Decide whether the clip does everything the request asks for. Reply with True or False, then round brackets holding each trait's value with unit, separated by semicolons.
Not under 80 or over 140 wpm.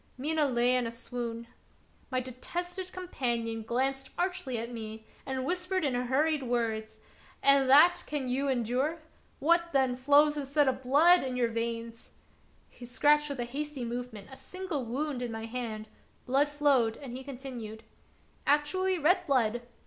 False (160 wpm)